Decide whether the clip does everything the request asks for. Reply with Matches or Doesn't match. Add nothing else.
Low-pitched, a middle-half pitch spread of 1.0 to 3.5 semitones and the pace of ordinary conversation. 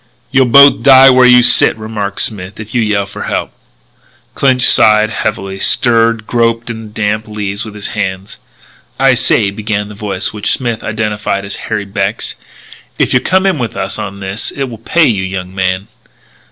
Matches